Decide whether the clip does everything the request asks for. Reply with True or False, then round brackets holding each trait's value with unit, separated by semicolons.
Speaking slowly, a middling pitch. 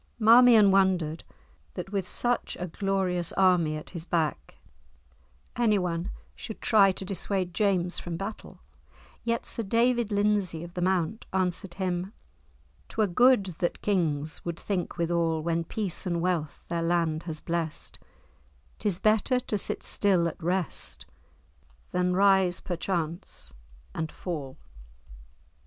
True (130 wpm; 180 Hz)